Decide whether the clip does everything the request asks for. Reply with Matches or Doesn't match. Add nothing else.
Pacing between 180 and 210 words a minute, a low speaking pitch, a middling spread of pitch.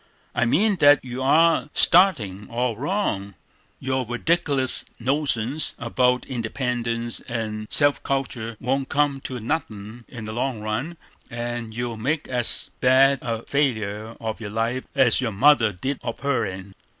Doesn't match